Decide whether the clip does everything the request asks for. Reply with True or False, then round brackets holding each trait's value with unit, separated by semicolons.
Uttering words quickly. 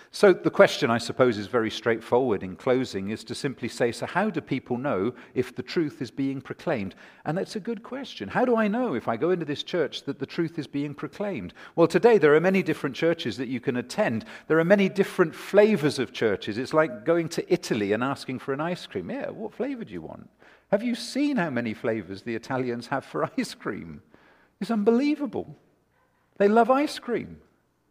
True (215 wpm)